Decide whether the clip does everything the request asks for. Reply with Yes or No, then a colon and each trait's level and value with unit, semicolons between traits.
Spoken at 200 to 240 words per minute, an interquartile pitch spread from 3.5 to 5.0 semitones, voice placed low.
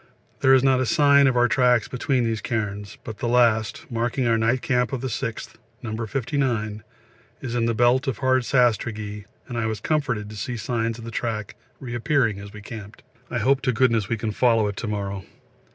No: fast, 205 wpm; average, 2.8 semitones; low, 115 Hz